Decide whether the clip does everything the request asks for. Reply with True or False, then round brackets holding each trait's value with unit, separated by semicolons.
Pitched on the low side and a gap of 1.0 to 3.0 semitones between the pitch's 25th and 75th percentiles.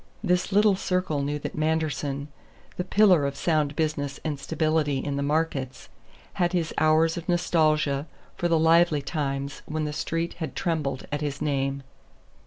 False (155 Hz; 2.7 semitones)